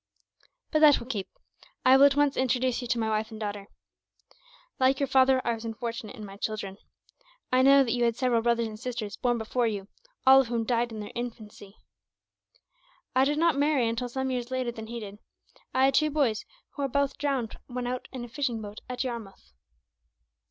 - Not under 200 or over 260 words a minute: Yes, fast, 205 wpm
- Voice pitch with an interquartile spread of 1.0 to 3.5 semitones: Yes, average, 3.0 semitones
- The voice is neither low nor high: No, high, 240 Hz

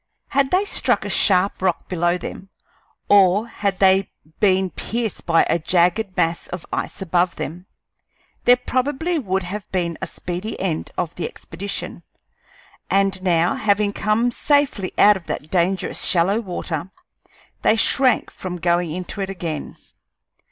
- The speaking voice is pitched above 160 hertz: Yes, high, 190 Hz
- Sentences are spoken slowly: No, average, 145 wpm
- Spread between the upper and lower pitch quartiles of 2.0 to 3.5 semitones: Yes, average, 3.2 semitones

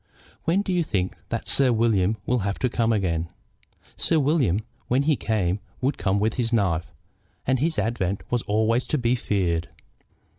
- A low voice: Yes, low, 115 Hz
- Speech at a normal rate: Yes, average, 175 wpm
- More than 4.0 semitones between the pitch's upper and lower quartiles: Yes, average, 4.8 semitones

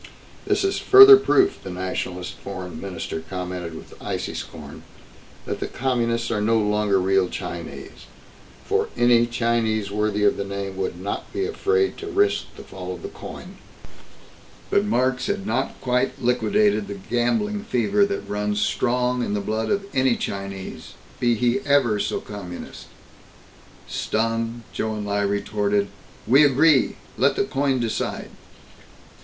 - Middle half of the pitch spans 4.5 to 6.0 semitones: Yes, average, 4.8 semitones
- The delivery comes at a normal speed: Yes, average, 150 wpm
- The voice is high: No, low, 115 Hz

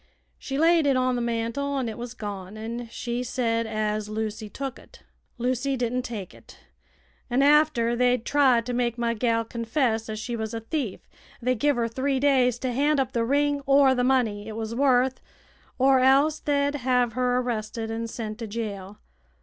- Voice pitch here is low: No, high, 245 Hz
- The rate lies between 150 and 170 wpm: No, average, 190 wpm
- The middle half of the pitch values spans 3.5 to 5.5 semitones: No, average, 2.8 semitones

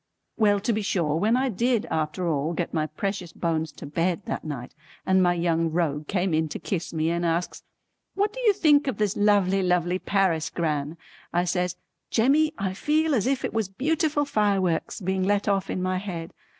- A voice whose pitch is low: No, medium, 185 Hz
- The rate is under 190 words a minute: No, average, 200 wpm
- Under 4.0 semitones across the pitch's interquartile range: No, average, 4.3 semitones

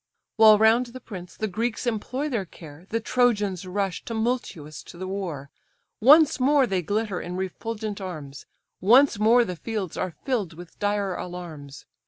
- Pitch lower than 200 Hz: No, high, 205 Hz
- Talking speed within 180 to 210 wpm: No, average, 160 wpm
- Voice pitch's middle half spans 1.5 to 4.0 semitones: No, average, 4.6 semitones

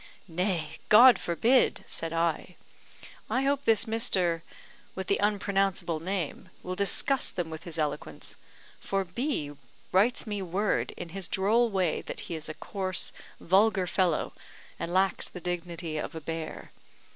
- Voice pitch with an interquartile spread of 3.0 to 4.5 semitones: Yes, average, 3.5 semitones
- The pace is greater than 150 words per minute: No, average, 145 wpm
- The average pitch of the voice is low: No, medium, 185 Hz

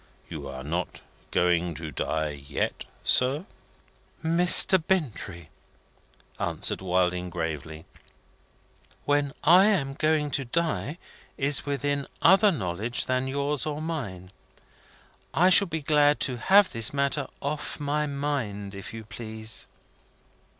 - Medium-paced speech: No, slow, 120 wpm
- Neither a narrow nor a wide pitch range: No, wide, 8.7 semitones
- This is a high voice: No, low, 135 Hz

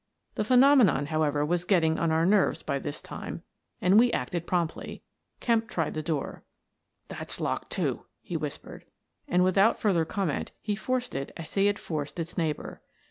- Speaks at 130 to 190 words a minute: Yes, average, 180 wpm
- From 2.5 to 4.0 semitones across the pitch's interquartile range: No, average, 4.6 semitones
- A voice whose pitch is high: No, medium, 175 Hz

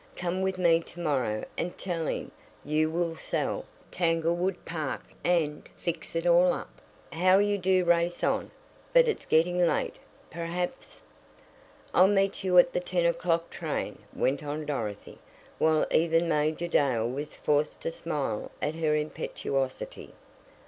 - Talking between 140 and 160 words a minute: Yes, average, 150 wpm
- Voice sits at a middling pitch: Yes, medium, 165 Hz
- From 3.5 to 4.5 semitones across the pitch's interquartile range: No, average, 2.8 semitones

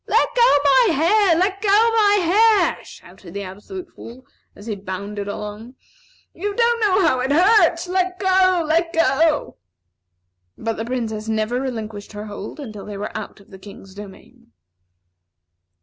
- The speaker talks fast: No, average, 155 wpm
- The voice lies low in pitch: No, very high, 270 Hz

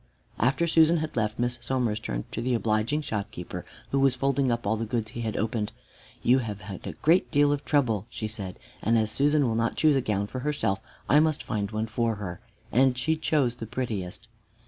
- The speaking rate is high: Yes, fast, 215 wpm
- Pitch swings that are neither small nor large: Yes, average, 4.3 semitones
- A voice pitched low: Yes, low, 115 Hz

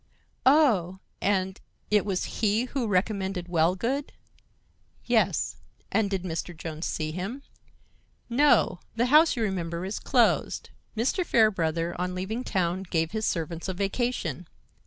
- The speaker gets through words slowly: Yes, slow, 130 wpm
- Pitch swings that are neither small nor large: Yes, average, 4.6 semitones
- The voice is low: No, high, 190 Hz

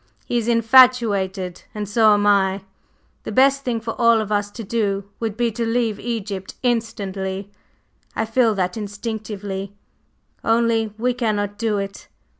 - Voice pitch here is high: Yes, high, 215 Hz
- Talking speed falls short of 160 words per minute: Yes, average, 150 wpm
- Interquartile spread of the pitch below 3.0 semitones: Yes, narrow, 2.5 semitones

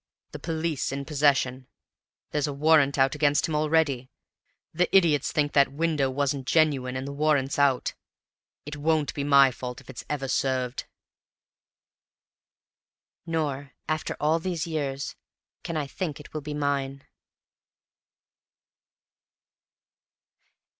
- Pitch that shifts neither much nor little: No, narrow, 2.3 semitones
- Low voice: No, medium, 145 Hz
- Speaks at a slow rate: Yes, slow, 125 wpm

